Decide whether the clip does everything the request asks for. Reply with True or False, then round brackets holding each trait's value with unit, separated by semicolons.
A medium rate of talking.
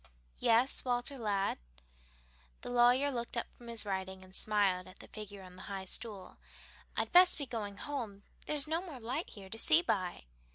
True (180 wpm)